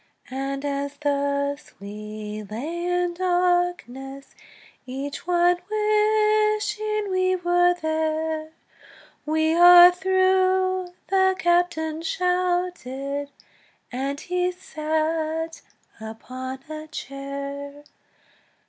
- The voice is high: Yes, very high, 320 Hz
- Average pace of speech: No, slow, 80 wpm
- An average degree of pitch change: Yes, average, 4.4 semitones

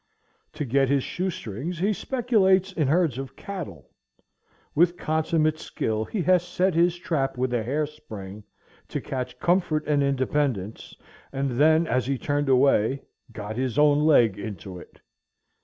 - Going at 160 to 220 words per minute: No, average, 150 wpm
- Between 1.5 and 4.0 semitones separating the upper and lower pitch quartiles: No, average, 5.2 semitones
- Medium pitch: Yes, medium, 145 Hz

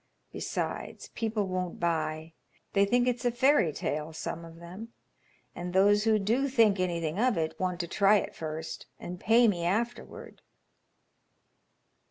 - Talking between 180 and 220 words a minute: No, average, 150 wpm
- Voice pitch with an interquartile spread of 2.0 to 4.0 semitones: No, average, 5.1 semitones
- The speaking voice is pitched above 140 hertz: Yes, high, 190 Hz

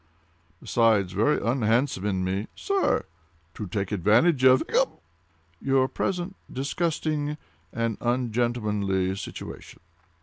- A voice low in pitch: Yes, low, 115 Hz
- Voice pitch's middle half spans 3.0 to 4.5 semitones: No, average, 5.1 semitones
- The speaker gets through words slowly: Yes, slow, 100 wpm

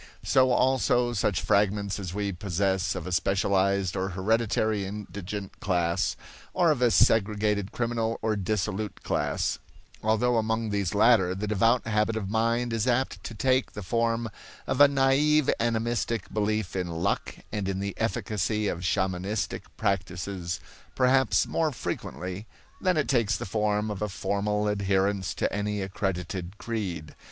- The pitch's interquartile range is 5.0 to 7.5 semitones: No, average, 3.2 semitones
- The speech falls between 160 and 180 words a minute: No, average, 145 wpm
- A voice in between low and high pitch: No, low, 105 Hz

